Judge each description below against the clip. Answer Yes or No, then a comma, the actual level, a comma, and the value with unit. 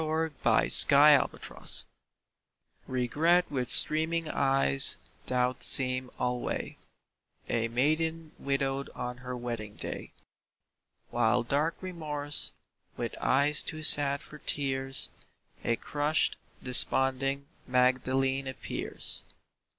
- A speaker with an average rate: No, slow, 95 wpm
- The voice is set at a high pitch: No, low, 135 Hz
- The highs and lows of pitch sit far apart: No, average, 3.0 semitones